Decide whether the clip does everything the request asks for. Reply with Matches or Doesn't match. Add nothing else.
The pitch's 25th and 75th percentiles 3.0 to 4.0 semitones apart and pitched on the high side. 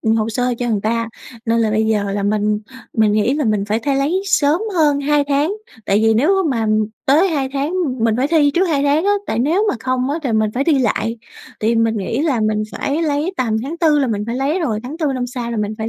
Doesn't match